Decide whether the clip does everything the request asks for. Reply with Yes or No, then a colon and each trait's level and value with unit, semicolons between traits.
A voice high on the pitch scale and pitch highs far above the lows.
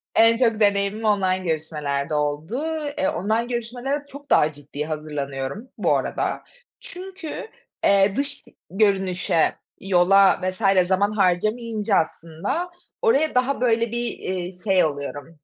Yes: high, 200 Hz; wide, 6.3 semitones